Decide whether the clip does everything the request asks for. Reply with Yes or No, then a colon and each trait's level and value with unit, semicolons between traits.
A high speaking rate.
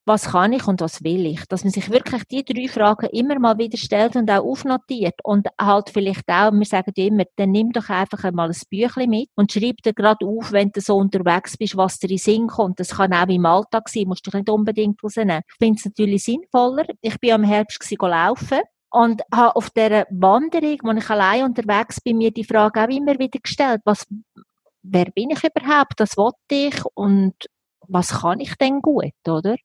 Yes: fast, 220 wpm